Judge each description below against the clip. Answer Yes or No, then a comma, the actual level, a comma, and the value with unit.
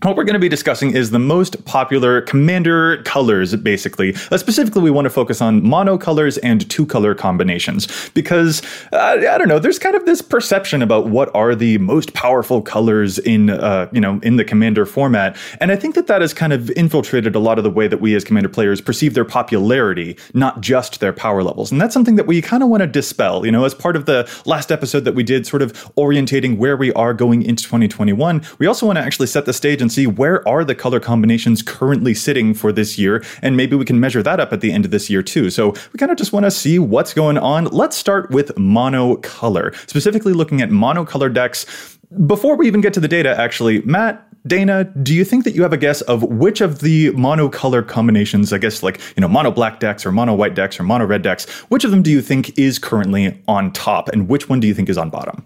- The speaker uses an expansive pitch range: Yes, wide, 7.3 semitones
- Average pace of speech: No, fast, 240 wpm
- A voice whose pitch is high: No, medium, 140 Hz